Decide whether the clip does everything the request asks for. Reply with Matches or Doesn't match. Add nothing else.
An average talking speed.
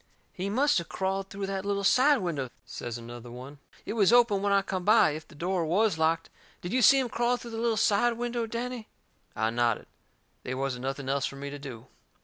Doesn't match